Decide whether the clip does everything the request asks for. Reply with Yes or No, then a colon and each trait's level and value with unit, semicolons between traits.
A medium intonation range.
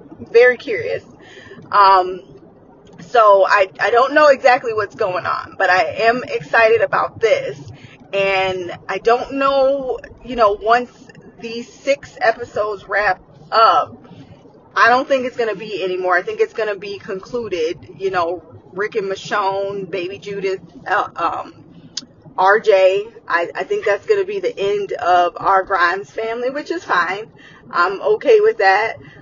No: wide, 6.6 semitones